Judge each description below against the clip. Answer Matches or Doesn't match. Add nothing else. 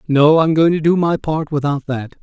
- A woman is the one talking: Doesn't match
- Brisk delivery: Matches